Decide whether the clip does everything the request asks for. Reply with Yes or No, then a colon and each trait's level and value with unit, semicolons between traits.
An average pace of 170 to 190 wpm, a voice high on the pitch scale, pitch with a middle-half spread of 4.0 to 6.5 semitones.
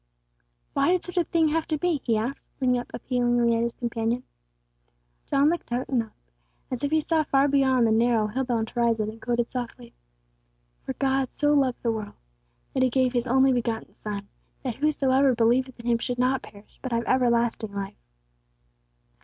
No: average, 185 wpm; high, 245 Hz; narrow, 2.6 semitones